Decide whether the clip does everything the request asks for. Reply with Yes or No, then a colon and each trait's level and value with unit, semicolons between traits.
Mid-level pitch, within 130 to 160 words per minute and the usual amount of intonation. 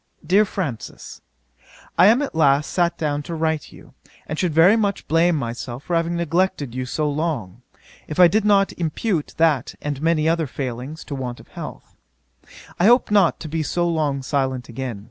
No: medium, 160 Hz; average, 185 wpm; average, 4.1 semitones